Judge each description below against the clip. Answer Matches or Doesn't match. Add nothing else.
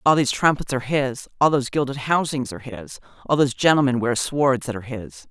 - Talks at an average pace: Doesn't match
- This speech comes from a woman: Matches